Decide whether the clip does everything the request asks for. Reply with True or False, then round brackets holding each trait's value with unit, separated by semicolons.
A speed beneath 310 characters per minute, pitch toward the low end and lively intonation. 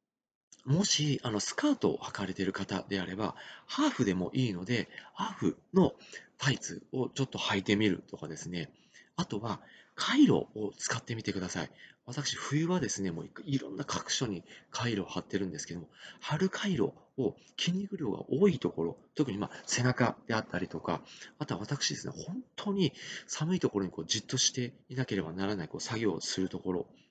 False (365 characters per minute; 120 Hz; 7.0 semitones)